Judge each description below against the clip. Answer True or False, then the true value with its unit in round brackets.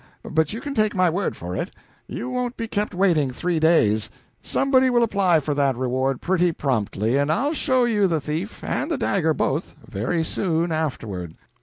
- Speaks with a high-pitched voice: False (165 Hz)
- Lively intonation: True (7.4 semitones)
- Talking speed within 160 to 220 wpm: True (185 wpm)